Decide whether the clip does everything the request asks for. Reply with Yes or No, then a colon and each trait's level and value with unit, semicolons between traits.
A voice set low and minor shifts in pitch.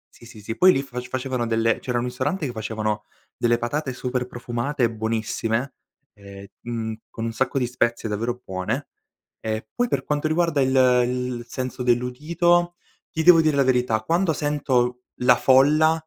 No: low, 125 Hz; average, 3.8 semitones